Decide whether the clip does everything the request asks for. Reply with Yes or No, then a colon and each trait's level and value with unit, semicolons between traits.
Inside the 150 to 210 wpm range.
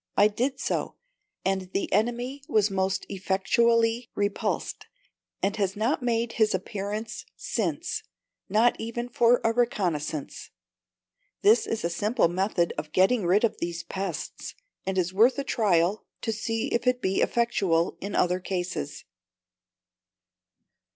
No: slow, 135 wpm